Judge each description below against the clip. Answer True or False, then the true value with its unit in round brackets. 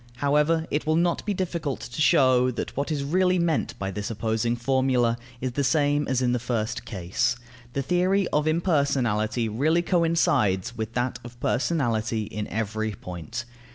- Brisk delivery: False (165 wpm)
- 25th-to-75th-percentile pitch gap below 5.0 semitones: False (5.6 semitones)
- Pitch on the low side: True (130 Hz)